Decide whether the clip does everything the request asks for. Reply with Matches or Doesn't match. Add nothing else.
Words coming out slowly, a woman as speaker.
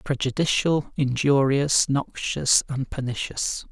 Doesn't match